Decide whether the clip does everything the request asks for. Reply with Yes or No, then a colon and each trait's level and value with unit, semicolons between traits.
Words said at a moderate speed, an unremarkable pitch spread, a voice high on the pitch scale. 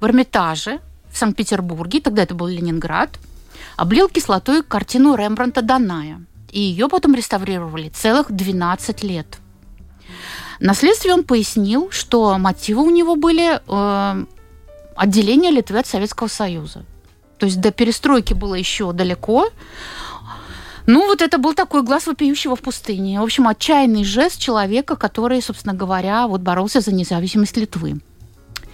No: average, 130 wpm; wide, 6.4 semitones; high, 210 Hz